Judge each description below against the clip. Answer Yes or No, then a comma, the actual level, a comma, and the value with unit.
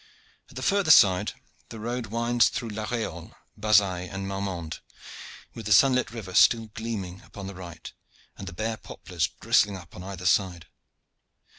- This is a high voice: No, low, 100 Hz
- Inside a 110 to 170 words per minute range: Yes, average, 160 wpm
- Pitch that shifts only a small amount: No, average, 3.8 semitones